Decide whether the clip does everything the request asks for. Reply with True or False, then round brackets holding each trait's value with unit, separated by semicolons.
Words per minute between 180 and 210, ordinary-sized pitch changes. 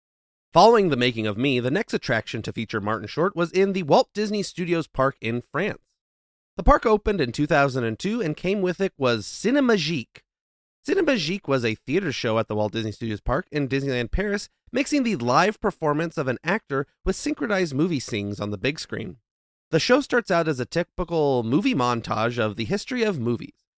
False (190 wpm; 8.5 semitones)